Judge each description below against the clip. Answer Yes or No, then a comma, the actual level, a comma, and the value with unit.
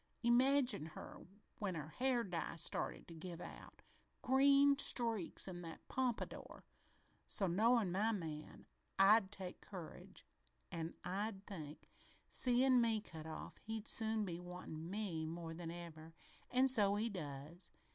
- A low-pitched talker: No, high, 195 Hz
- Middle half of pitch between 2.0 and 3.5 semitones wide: No, wide, 5.6 semitones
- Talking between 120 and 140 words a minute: Yes, slow, 135 wpm